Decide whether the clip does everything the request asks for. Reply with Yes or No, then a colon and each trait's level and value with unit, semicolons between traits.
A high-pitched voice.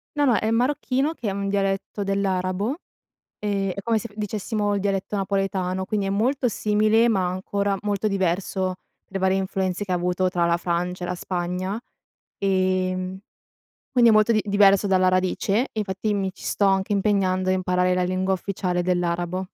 Yes: high, 195 Hz